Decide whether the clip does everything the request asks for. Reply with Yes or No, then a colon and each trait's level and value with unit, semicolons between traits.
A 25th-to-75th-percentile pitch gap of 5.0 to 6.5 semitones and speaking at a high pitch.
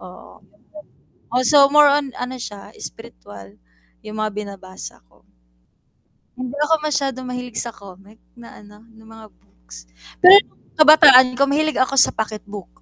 Yes: wide, 5.4 semitones; high, 240 Hz